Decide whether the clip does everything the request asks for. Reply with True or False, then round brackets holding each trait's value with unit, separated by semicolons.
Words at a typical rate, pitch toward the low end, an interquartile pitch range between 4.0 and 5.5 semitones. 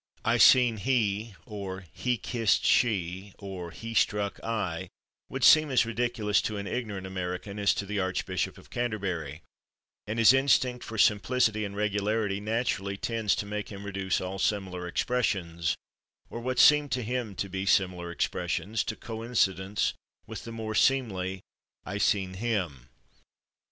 False (150 wpm; 105 Hz; 3.3 semitones)